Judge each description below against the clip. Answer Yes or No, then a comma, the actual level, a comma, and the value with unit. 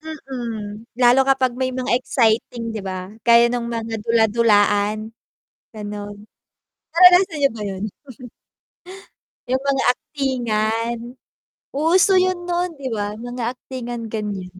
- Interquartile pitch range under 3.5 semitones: No, average, 3.8 semitones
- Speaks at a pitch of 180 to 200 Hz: No, high, 235 Hz